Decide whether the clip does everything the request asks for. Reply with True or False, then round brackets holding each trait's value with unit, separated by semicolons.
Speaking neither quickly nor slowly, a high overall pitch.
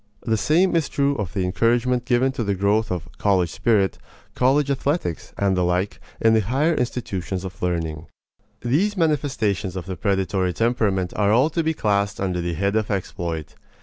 False (180 wpm; 105 Hz)